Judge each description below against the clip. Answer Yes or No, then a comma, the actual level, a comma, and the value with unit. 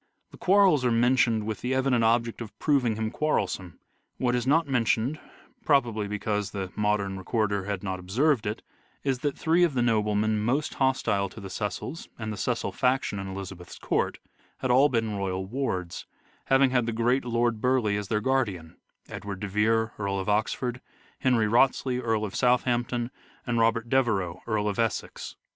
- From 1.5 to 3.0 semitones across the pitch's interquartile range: No, average, 3.7 semitones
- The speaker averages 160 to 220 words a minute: Yes, average, 180 wpm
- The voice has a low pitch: Yes, low, 115 Hz